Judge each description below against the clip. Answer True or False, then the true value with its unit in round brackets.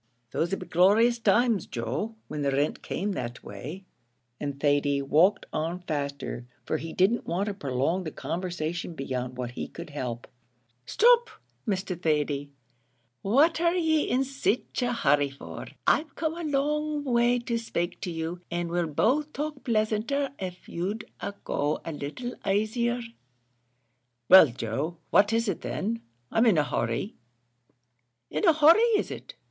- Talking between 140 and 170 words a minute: True (155 wpm)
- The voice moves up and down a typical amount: False (8.3 semitones)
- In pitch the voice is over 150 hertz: True (185 Hz)